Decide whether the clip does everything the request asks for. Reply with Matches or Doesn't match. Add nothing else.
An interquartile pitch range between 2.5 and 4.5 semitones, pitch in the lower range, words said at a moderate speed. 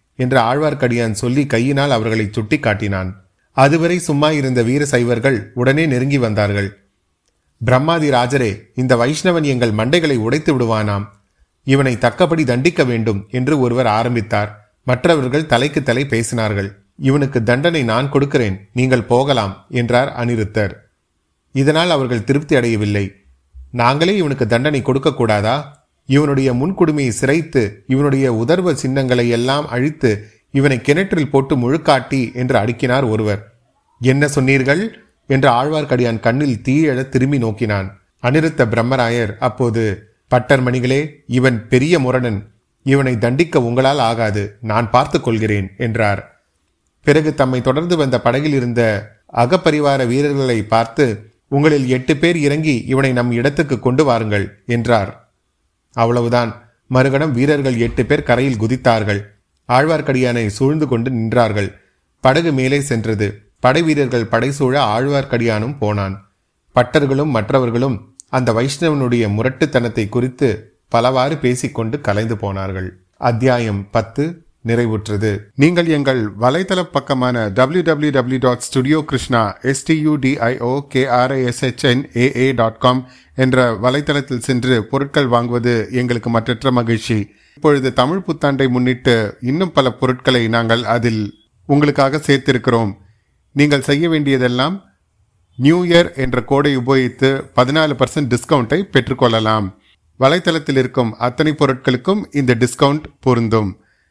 Matches